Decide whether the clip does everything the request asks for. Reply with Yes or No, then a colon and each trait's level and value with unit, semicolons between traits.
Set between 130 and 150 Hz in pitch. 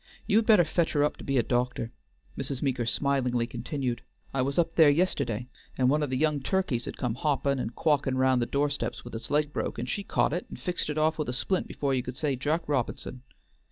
Yes: medium, 140 Hz